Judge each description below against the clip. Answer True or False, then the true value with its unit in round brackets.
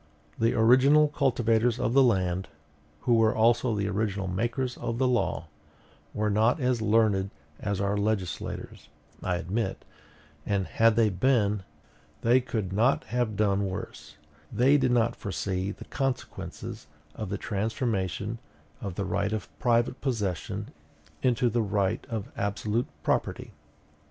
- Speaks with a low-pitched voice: True (110 Hz)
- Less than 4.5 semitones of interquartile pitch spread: True (3.4 semitones)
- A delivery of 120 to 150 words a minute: True (135 wpm)